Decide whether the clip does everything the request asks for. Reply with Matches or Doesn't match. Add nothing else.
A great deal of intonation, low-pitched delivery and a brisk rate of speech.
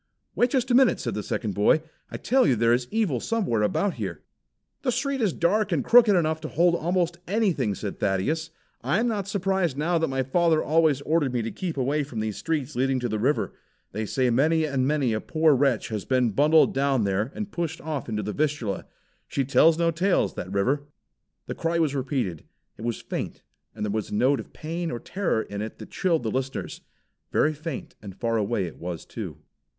Doesn't match